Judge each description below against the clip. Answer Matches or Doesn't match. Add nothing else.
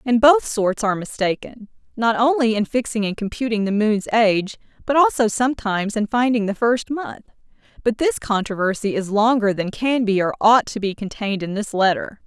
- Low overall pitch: Doesn't match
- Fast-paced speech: Doesn't match